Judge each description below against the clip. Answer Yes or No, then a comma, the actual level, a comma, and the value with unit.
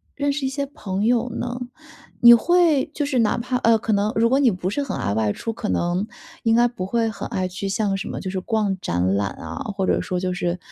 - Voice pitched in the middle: No, high, 220 Hz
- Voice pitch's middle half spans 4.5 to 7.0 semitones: Yes, average, 4.9 semitones